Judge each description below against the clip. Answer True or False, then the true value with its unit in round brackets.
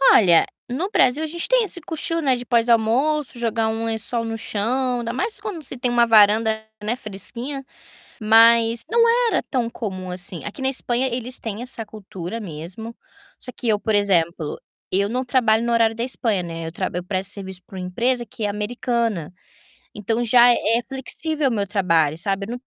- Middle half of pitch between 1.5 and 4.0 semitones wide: True (3.7 semitones)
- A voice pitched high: True (230 Hz)